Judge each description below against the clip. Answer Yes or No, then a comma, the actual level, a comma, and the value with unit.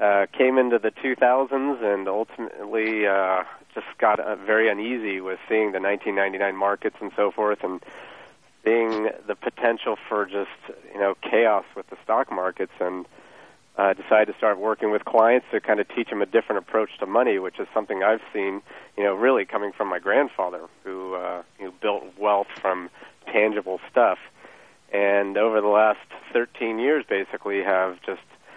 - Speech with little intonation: Yes, narrow, 2.1 semitones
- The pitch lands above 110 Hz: No, low, 100 Hz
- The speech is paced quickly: No, average, 170 wpm